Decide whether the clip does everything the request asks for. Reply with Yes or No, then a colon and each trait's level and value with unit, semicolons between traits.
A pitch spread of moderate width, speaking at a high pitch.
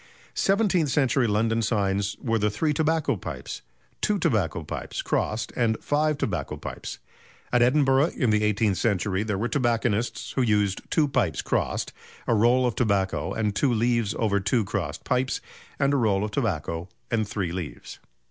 No: average, 4.3 semitones; low, 115 Hz